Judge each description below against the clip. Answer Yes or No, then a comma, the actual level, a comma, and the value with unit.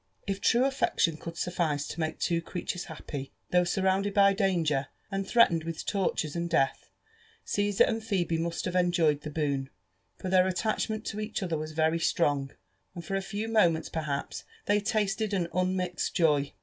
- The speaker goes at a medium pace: Yes, average, 175 wpm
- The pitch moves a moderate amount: Yes, average, 3.7 semitones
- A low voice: No, medium, 175 Hz